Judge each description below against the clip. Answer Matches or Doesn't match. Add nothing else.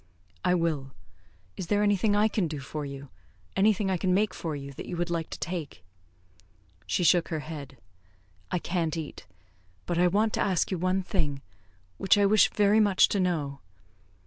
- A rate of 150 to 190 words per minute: Matches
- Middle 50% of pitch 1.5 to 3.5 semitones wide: Doesn't match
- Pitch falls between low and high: Matches